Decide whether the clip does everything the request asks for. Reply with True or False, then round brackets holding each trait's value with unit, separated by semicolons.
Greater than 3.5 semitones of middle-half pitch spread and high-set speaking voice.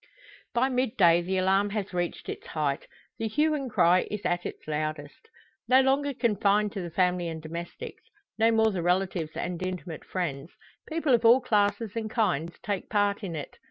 True (4.7 semitones; 195 Hz)